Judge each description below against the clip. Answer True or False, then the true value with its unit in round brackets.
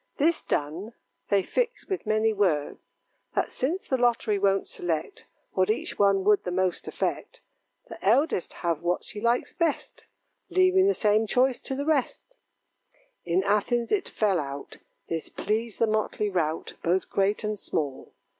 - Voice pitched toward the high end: True (210 Hz)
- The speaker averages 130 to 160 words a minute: True (155 wpm)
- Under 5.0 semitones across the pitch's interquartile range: False (5.3 semitones)